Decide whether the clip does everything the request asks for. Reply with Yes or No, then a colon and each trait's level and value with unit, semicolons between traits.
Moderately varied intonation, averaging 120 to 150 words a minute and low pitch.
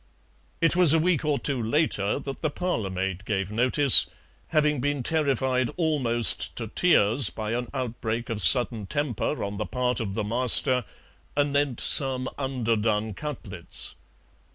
Yes: average, 4.7 semitones; average, 145 wpm; low, 125 Hz